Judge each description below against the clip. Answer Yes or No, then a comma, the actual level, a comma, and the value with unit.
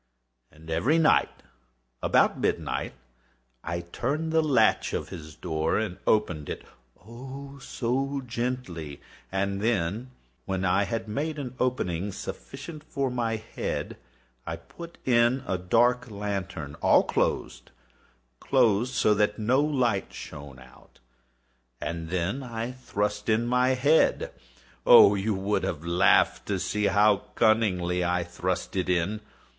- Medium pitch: No, low, 105 Hz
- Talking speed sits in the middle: No, slow, 130 wpm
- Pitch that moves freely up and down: Yes, wide, 5.9 semitones